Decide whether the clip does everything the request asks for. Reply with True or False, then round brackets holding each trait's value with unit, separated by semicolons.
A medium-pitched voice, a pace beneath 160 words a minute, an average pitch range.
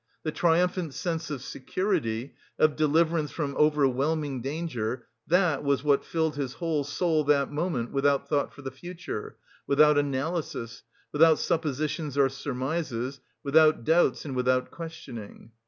True (145 Hz; 135 wpm; 3.3 semitones)